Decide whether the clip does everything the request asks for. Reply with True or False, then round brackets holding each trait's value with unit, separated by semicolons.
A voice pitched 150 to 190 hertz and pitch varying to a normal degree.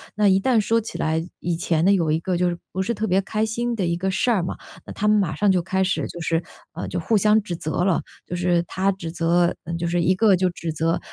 True (185 Hz; 3.2 semitones)